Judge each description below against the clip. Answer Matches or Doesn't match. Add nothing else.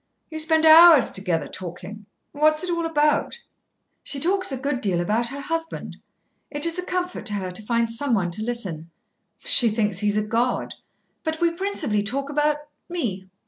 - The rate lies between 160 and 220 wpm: Matches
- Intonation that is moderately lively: Doesn't match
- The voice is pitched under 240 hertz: Doesn't match